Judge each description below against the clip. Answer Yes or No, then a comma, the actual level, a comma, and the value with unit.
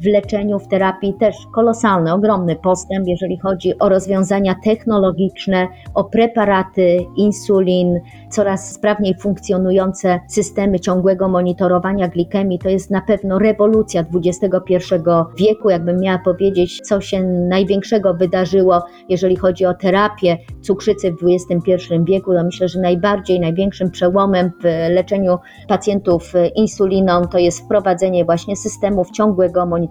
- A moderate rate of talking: Yes, average, 125 wpm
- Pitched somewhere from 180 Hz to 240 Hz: Yes, high, 190 Hz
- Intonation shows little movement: Yes, narrow, 1.9 semitones